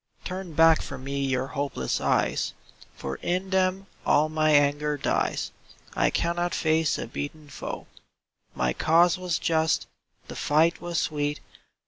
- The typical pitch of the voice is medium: Yes, medium, 155 Hz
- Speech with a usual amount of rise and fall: Yes, average, 3.1 semitones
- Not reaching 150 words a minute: Yes, average, 140 wpm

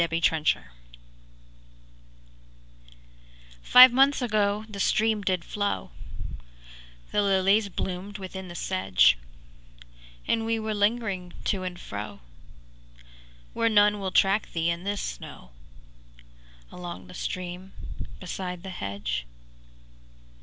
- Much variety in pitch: No, average, 3.5 semitones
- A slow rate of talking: Yes, slow, 105 wpm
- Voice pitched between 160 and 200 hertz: Yes, high, 190 Hz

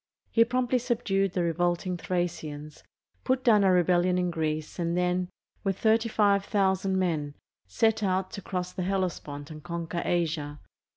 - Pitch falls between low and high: Yes, medium, 180 Hz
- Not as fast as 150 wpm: Yes, average, 140 wpm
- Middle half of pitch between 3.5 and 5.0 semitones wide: No, average, 2.7 semitones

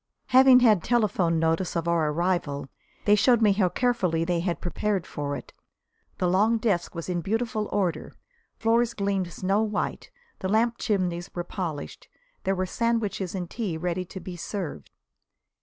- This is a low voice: No, medium, 185 Hz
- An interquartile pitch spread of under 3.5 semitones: No, average, 4.0 semitones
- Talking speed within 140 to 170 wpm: Yes, average, 160 wpm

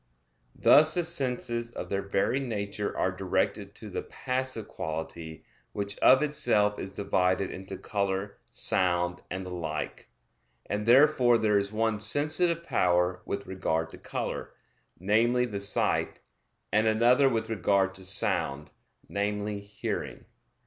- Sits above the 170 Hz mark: No, low, 105 Hz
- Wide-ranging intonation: No, average, 4.1 semitones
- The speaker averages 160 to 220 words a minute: No, slow, 135 wpm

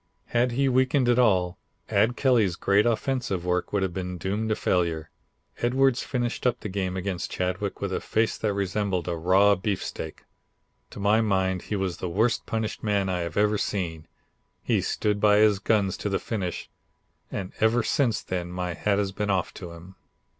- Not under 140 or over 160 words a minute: No, average, 185 wpm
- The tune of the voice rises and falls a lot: No, average, 3.4 semitones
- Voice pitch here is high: No, low, 100 Hz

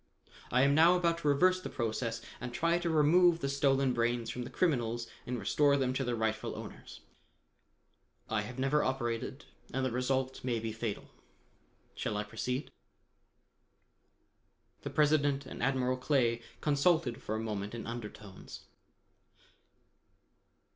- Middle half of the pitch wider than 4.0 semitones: No, average, 3.7 semitones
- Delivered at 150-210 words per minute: No, average, 140 wpm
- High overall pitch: No, low, 130 Hz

